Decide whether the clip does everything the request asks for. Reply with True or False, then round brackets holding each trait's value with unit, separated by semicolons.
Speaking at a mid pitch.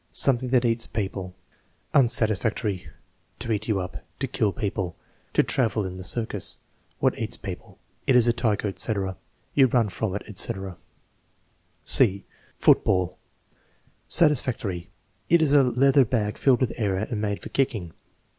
False (110 Hz)